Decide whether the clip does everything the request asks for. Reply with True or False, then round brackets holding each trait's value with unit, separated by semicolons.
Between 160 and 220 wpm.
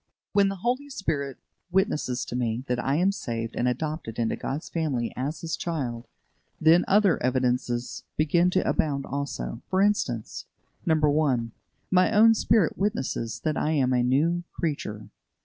False (150 wpm)